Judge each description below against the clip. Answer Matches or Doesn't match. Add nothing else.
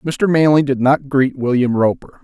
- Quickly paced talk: Doesn't match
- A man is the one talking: Matches